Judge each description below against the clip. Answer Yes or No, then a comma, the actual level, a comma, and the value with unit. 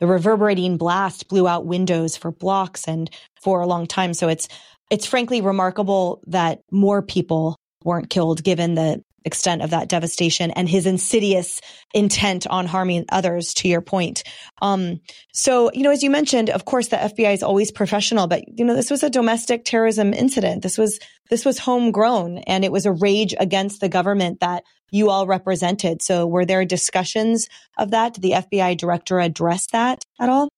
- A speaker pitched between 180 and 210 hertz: Yes, high, 190 Hz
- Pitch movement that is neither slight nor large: Yes, average, 3.6 semitones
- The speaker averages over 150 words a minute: Yes, average, 180 wpm